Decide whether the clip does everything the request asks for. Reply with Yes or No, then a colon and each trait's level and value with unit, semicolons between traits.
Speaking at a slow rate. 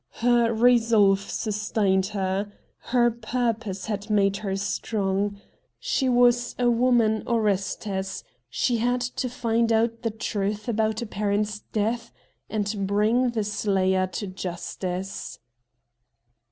Yes: slow, 120 wpm